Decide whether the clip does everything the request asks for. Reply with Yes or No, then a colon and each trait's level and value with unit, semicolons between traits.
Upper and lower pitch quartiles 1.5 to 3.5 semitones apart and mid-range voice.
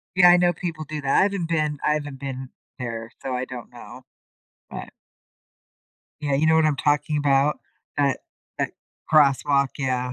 Yes: narrow, 2.6 semitones; medium, 145 Hz